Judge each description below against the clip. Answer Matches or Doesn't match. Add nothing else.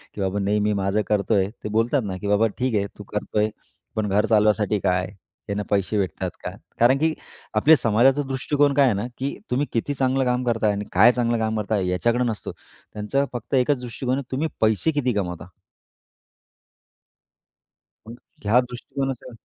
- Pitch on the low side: Matches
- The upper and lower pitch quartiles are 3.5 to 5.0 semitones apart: Matches